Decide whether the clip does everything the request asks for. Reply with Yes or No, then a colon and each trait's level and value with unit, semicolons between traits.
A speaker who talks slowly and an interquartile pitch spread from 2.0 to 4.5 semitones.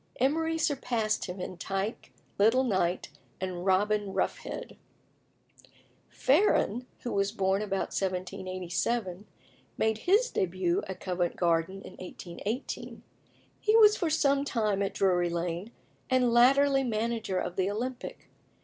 No: slow, 120 wpm; wide, 5.4 semitones